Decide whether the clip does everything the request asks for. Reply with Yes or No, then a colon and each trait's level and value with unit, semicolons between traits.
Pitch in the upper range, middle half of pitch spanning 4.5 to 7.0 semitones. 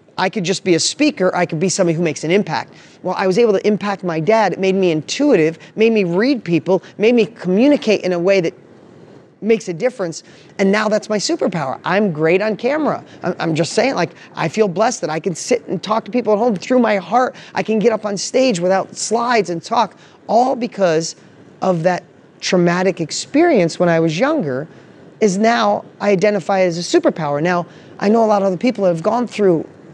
No: high, 195 Hz; average, 3.8 semitones